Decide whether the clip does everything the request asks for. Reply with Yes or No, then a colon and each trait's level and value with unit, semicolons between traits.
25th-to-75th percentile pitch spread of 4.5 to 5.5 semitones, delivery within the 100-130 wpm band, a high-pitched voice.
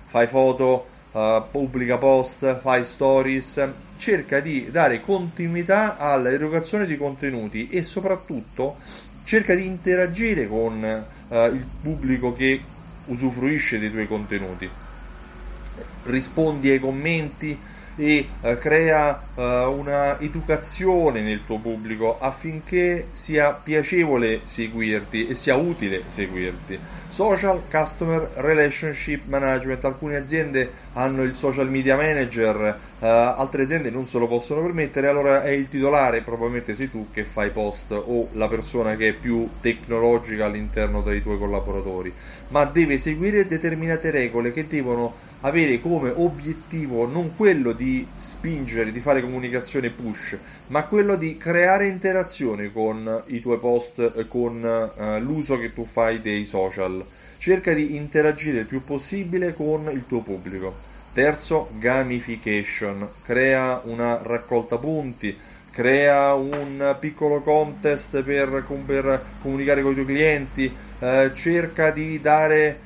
No: average, 4.9 semitones; average, 125 wpm; low, 135 Hz